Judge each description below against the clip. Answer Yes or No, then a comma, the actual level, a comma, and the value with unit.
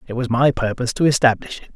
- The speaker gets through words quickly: Yes, fast, 240 wpm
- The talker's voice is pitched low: Yes, low, 125 Hz